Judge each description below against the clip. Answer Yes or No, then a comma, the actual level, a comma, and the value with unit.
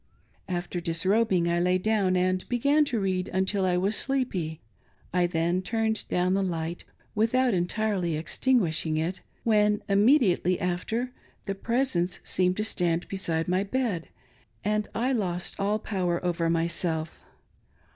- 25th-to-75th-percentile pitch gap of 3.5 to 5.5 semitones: Yes, average, 3.9 semitones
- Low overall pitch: No, medium, 185 Hz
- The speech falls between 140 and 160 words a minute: Yes, average, 145 wpm